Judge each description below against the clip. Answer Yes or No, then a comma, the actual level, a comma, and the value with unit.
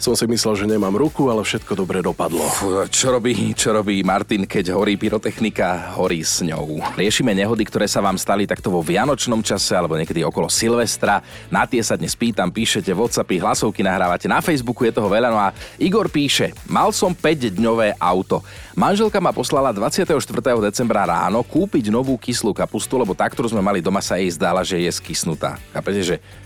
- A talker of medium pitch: No, low, 115 Hz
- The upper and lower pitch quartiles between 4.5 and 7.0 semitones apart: Yes, average, 5.1 semitones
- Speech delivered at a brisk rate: Yes, fast, 185 wpm